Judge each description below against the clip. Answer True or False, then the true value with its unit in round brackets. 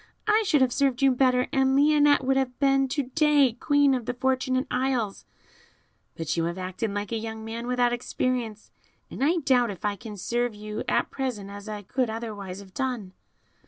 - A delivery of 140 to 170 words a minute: False (195 wpm)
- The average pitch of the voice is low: False (245 Hz)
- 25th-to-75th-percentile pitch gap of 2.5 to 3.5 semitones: False (4.0 semitones)